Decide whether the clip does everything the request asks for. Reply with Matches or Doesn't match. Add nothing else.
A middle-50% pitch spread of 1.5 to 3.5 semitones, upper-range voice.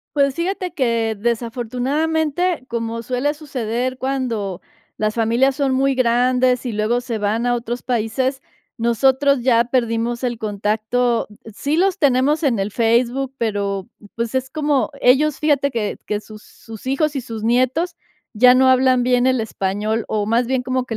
Matches